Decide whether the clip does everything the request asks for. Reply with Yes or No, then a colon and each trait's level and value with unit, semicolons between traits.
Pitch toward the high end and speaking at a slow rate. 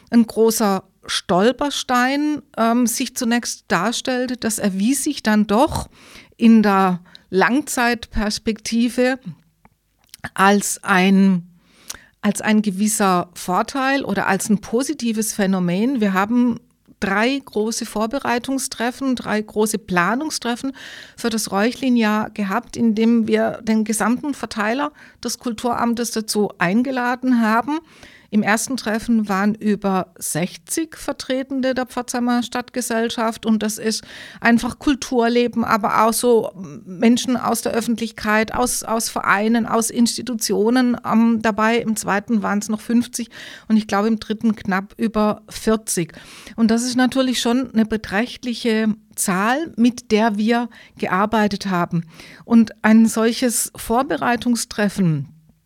Yes: high, 225 Hz; slow, 115 wpm